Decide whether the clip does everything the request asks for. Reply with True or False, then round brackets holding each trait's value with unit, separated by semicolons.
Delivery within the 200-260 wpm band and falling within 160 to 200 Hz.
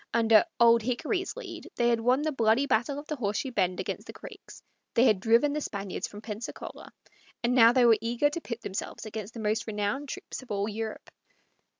False (205 wpm; 230 Hz)